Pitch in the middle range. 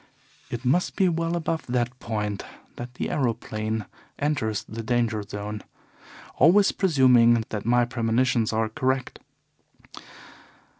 No: low, 120 Hz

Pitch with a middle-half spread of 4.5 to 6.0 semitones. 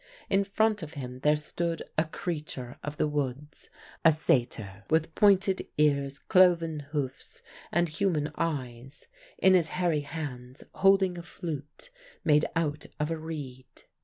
No: average, 3.4 semitones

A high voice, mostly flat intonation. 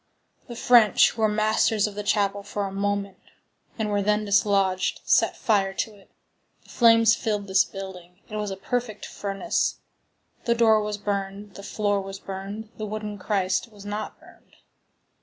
Yes: high, 205 Hz; narrow, 1.6 semitones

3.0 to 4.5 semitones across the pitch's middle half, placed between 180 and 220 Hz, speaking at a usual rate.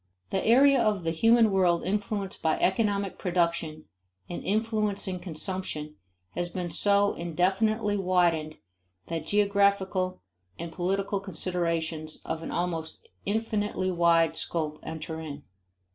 No: average, 3.4 semitones; medium, 185 Hz; slow, 115 wpm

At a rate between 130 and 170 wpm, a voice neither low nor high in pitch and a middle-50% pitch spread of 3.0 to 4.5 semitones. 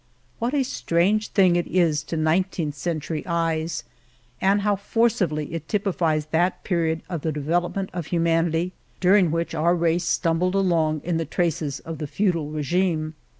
No: average, 165 wpm; medium, 170 Hz; narrow, 2.5 semitones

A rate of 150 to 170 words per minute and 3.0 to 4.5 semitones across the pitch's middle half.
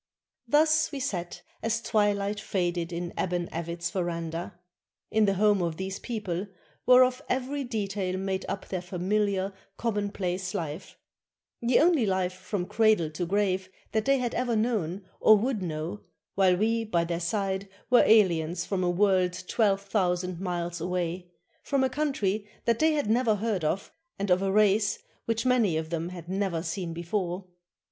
Yes: average, 165 wpm; average, 3.6 semitones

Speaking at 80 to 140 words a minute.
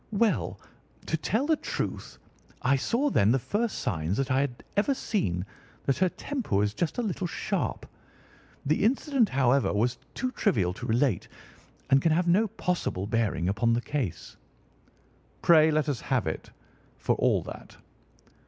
No: average, 160 wpm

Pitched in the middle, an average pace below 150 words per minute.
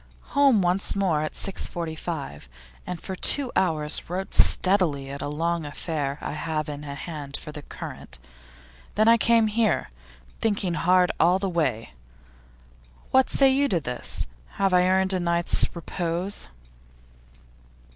Yes: medium, 175 Hz; average, 140 wpm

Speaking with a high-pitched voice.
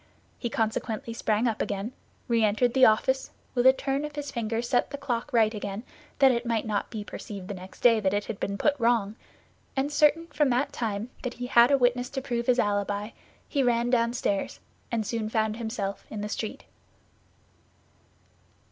Yes: high, 235 Hz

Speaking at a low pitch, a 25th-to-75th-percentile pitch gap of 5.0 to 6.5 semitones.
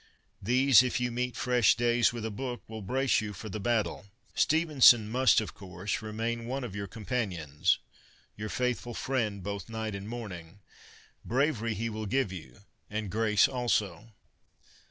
No: low, 110 Hz; average, 3.2 semitones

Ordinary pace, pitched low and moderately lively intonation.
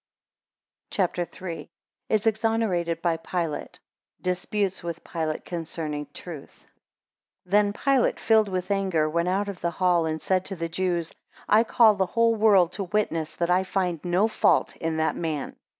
No: average, 165 wpm; medium, 180 Hz; average, 3.4 semitones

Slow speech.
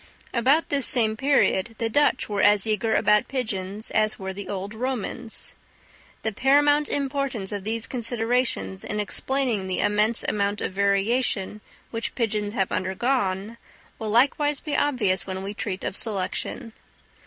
No: average, 145 wpm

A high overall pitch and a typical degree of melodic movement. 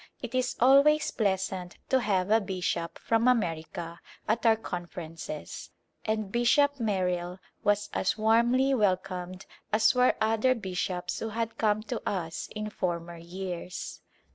Yes: high, 205 Hz; average, 4.3 semitones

